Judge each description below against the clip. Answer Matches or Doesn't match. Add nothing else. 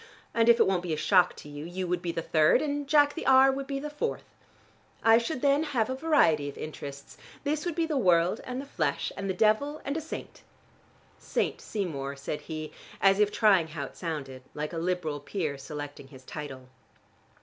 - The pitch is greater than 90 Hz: Matches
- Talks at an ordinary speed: Doesn't match